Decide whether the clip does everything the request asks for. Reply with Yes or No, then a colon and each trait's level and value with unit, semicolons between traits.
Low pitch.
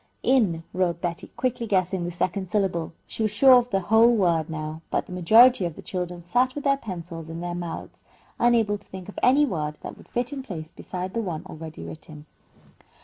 No: medium, 185 Hz